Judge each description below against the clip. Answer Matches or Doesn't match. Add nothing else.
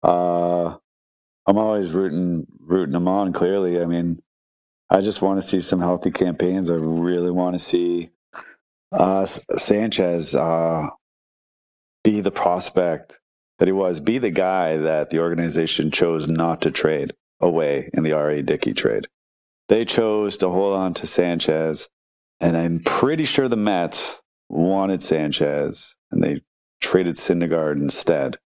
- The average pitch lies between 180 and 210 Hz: Doesn't match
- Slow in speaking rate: Doesn't match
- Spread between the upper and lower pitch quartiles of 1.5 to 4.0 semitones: Matches